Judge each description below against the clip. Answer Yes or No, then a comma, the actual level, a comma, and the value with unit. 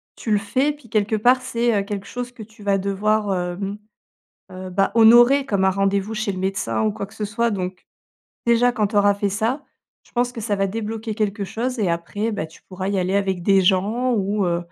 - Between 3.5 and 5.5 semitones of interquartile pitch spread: No, average, 2.9 semitones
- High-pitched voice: Yes, high, 205 Hz